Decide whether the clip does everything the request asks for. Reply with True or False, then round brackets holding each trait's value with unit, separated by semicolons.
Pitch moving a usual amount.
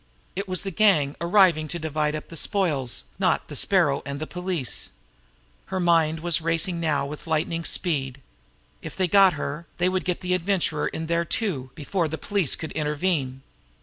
True (3.3 semitones)